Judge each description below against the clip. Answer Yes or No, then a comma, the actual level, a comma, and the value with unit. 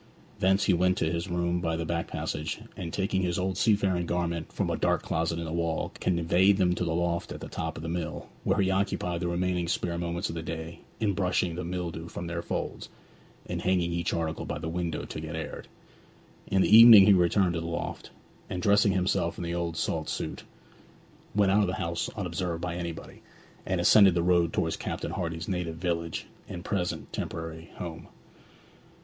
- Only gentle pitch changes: Yes, narrow, 1.8 semitones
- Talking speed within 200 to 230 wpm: Yes, fast, 205 wpm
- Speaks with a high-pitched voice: No, very low, 85 Hz